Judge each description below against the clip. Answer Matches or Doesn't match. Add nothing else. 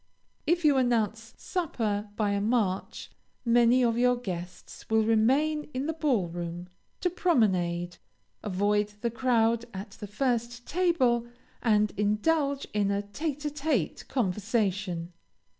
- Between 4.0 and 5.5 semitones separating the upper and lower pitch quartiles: Matches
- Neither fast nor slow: Doesn't match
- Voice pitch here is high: Matches